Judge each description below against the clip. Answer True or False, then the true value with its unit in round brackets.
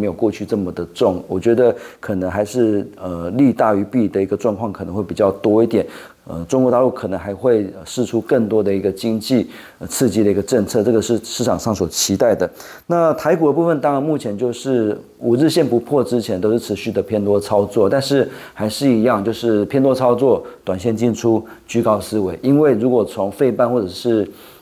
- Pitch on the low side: True (115 Hz)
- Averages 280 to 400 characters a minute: True (310 characters per minute)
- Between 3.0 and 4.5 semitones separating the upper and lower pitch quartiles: True (3.6 semitones)